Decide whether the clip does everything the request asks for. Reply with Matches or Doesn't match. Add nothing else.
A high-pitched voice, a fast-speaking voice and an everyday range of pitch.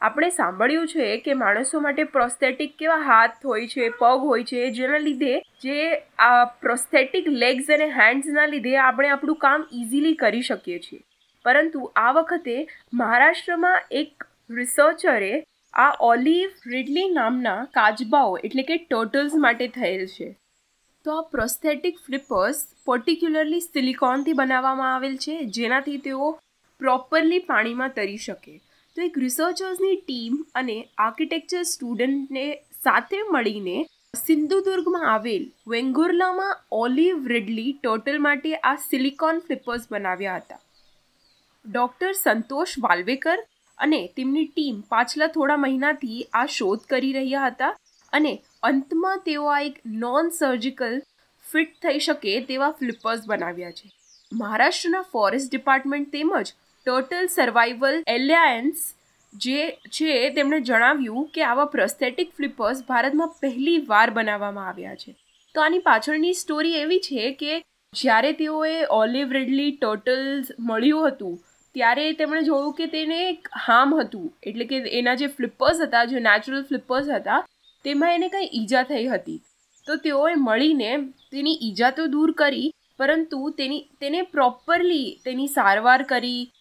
Doesn't match